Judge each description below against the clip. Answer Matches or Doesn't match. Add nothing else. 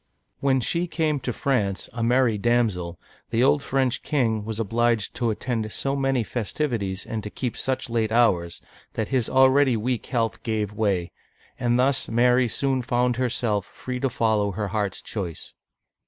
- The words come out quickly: Doesn't match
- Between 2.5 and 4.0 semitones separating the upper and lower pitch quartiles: Matches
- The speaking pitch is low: Matches